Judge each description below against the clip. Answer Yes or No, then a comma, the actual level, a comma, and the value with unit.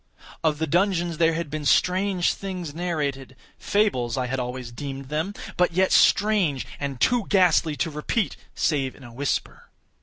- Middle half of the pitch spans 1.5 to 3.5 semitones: No, average, 5.0 semitones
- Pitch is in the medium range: Yes, medium, 160 Hz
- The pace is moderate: Yes, average, 150 wpm